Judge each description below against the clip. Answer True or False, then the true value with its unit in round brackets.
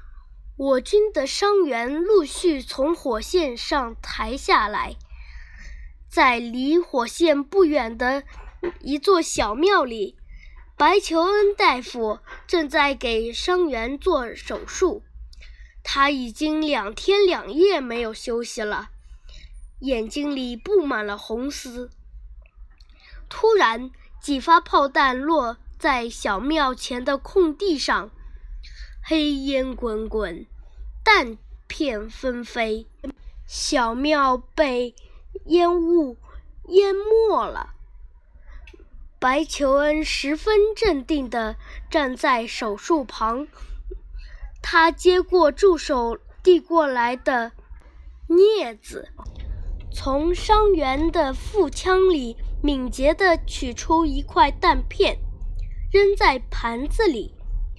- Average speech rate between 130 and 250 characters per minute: True (140 characters per minute)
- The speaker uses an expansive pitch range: True (6.8 semitones)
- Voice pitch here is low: False (280 Hz)